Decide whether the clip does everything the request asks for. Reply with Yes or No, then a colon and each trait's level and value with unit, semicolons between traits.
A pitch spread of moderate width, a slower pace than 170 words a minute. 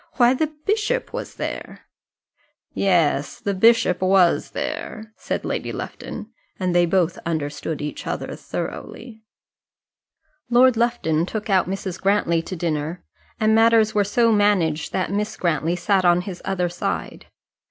Yes: average, 4.2 semitones; average, 140 wpm